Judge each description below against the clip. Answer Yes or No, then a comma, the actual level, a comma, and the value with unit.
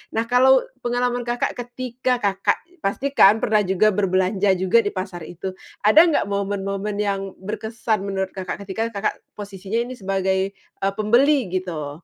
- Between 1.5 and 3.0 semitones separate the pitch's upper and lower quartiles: No, average, 3.6 semitones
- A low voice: No, high, 200 Hz